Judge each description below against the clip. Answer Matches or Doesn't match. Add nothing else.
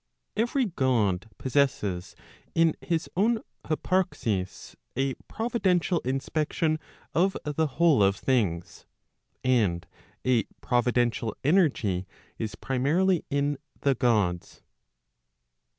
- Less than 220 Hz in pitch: Matches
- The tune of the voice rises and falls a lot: Matches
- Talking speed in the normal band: Doesn't match